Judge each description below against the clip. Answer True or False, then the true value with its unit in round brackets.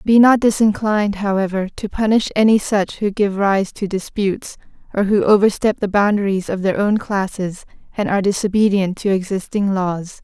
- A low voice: False (200 Hz)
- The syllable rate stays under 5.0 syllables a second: False (5.1 syllables/s)